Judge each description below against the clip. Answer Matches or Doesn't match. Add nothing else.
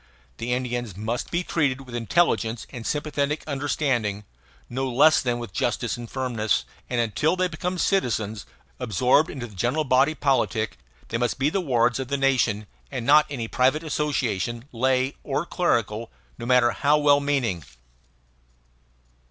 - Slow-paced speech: Doesn't match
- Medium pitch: Doesn't match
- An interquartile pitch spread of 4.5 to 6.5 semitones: Doesn't match